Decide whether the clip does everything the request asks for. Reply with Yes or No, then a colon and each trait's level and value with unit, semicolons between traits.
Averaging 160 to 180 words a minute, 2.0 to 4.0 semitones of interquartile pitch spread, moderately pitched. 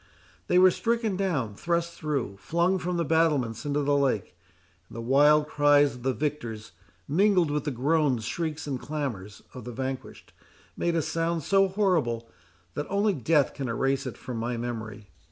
No: average, 170 wpm; wide, 5.4 semitones; medium, 145 Hz